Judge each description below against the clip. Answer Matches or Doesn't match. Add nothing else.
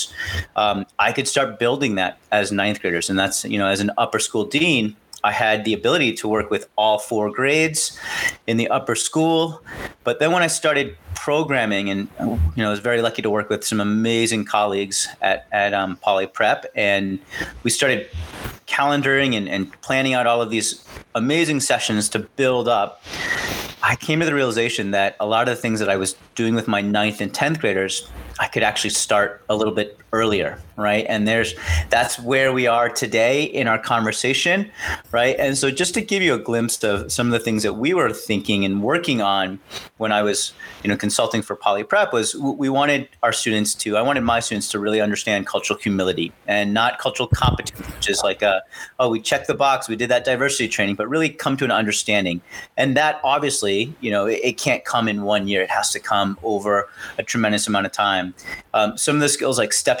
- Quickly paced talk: Matches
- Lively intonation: Doesn't match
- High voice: Doesn't match